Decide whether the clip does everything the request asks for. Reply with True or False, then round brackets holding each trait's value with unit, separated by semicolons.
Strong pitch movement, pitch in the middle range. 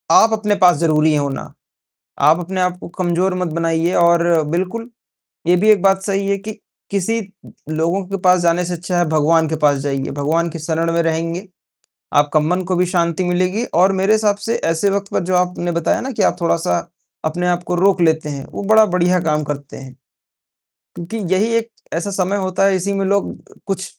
False (3.0 semitones; 180 Hz)